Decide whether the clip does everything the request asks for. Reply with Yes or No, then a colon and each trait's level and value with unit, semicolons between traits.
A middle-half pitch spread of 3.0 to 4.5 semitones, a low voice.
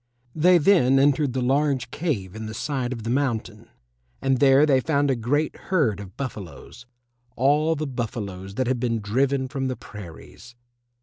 Yes: average, 3.8 semitones; low, 130 Hz